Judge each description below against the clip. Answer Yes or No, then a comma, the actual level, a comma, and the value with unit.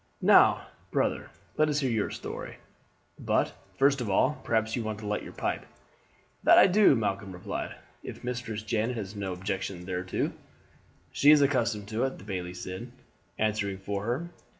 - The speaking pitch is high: No, low, 110 Hz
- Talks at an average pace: Yes, average, 170 wpm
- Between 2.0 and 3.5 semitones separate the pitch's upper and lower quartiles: No, average, 4.3 semitones